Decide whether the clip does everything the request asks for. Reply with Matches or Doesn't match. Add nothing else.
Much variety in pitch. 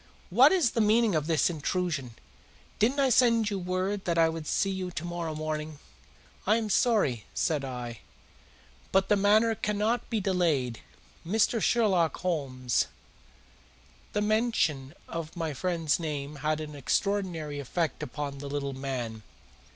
Matches